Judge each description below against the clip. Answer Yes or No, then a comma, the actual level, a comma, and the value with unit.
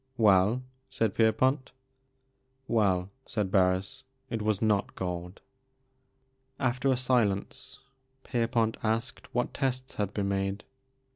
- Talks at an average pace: No, slow, 120 wpm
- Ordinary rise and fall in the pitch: Yes, average, 4.6 semitones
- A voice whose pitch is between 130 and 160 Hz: No, low, 110 Hz